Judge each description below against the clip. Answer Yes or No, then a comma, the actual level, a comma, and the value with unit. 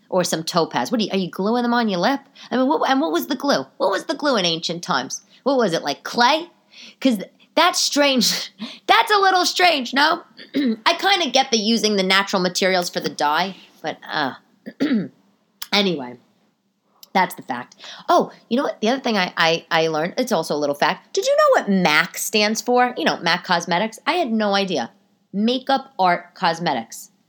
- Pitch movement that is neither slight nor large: No, wide, 6.7 semitones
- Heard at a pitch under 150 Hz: No, high, 215 Hz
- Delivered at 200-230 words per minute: Yes, fast, 205 wpm